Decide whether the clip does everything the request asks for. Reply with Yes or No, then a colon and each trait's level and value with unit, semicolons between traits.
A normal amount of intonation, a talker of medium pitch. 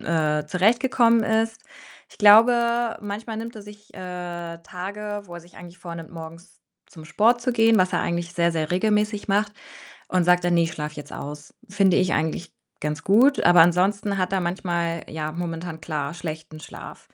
Yes: average, 4.0 semitones; medium, 180 Hz